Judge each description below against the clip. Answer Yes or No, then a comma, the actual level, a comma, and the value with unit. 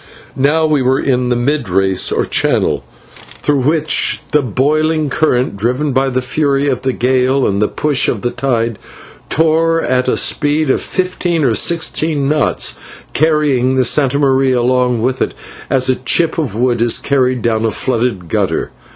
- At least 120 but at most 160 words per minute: No, average, 170 wpm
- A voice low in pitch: Yes, low, 130 Hz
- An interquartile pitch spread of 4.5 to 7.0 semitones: No, average, 3.3 semitones